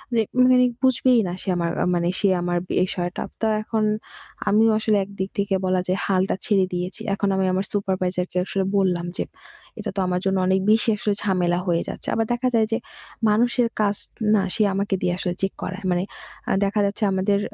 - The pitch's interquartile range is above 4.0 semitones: No, narrow, 2.6 semitones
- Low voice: No, high, 195 Hz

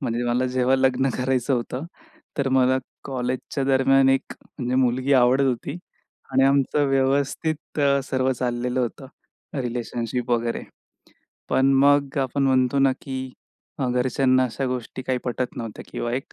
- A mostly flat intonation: Yes, narrow, 1.5 semitones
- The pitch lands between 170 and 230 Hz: No, low, 130 Hz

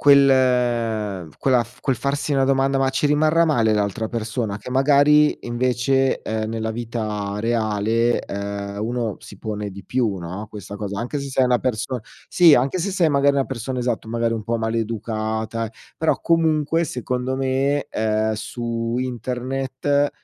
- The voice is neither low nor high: No, low, 120 Hz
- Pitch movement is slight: No, average, 3.6 semitones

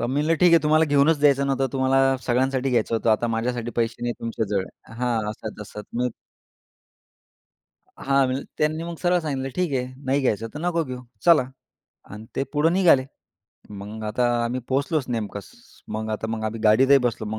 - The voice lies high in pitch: No, low, 130 Hz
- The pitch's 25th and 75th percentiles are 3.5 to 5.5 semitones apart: Yes, average, 4.3 semitones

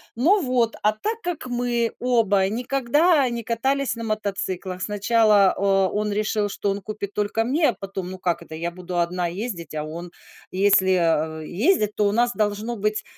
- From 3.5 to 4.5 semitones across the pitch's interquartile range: Yes, average, 4.1 semitones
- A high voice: Yes, high, 210 Hz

